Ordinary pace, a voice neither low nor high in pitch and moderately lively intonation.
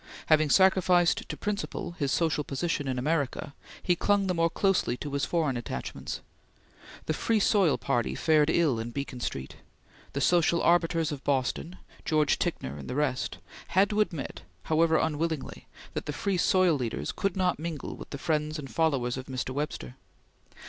Yes: average, 170 wpm; medium, 155 Hz; average, 4.2 semitones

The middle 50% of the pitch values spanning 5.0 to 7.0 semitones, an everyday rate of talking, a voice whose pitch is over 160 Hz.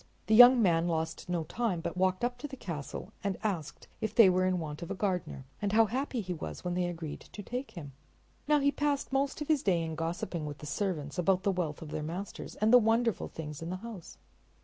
No: wide, 5.6 semitones; fast, 240 wpm; medium, 185 Hz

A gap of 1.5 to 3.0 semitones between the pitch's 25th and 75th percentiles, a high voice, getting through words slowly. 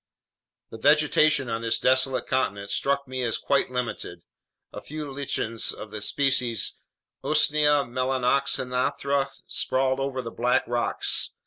No: narrow, 2.6 semitones; low, 130 Hz; slow, 125 wpm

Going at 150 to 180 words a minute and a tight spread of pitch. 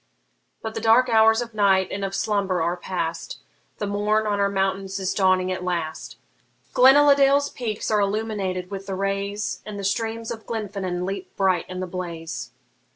No: average, 170 wpm; average, 3.0 semitones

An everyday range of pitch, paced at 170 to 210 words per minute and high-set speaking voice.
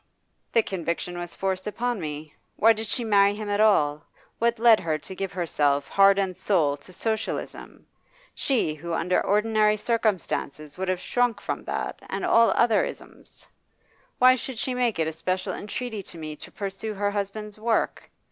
Yes: average, 4.3 semitones; average, 175 wpm; high, 200 Hz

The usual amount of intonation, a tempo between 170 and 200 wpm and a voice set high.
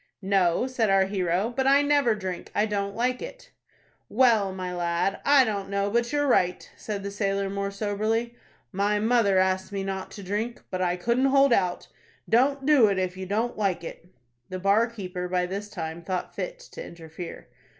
Yes: average, 4.0 semitones; average, 190 wpm; high, 200 Hz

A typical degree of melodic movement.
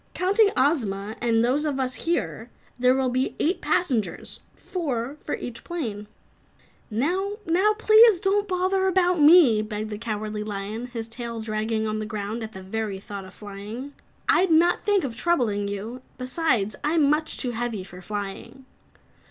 No: wide, 7.1 semitones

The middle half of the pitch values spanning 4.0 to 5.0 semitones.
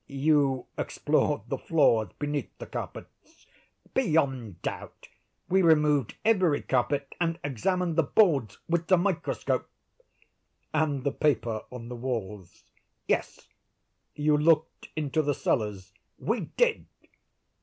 Yes: average, 4.6 semitones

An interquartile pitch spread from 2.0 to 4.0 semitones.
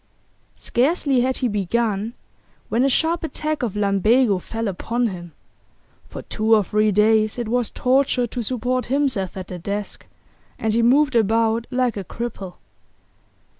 Yes: average, 3.4 semitones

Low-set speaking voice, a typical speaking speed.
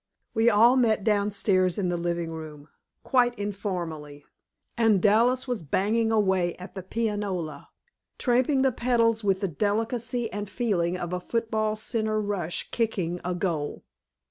No: high, 205 Hz; average, 145 wpm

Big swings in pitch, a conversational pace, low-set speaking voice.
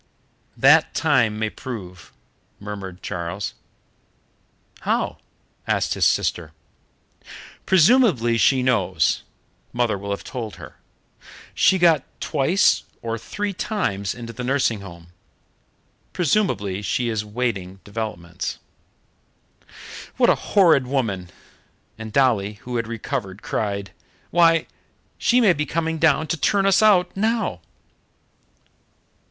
No: wide, 8.3 semitones; slow, 110 wpm; low, 120 Hz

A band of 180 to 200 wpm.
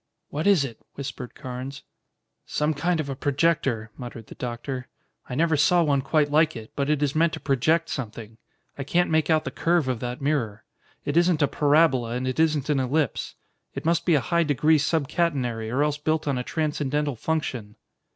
Yes: average, 195 wpm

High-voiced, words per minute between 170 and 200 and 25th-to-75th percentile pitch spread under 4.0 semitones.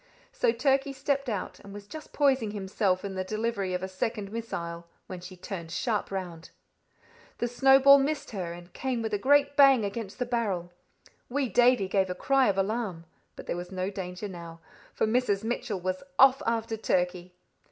No: high, 205 Hz; average, 185 wpm; average, 5.1 semitones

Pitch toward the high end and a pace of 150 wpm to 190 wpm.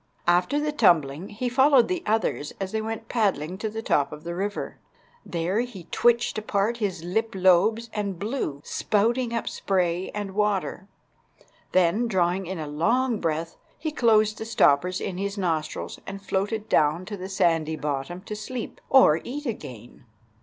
Yes: high, 195 Hz; average, 165 wpm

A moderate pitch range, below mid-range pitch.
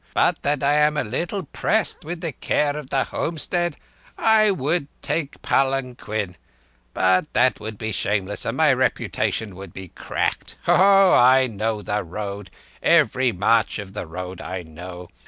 No: wide, 7.2 semitones; low, 125 Hz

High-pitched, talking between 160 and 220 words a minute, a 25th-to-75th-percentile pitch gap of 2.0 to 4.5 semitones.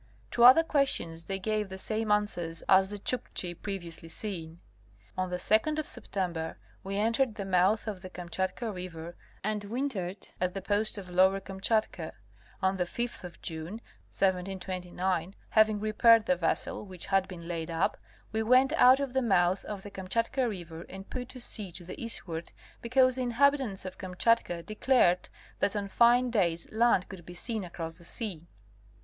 Yes: high, 195 Hz; average, 180 wpm; average, 4.1 semitones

